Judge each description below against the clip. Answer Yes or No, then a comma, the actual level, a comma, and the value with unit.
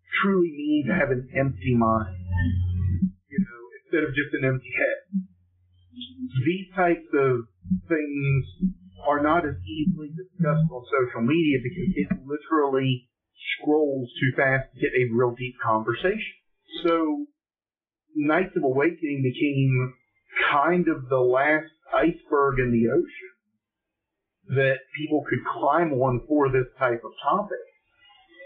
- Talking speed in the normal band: No, slow, 130 wpm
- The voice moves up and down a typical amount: No, wide, 6.4 semitones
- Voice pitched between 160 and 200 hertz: No, medium, 140 Hz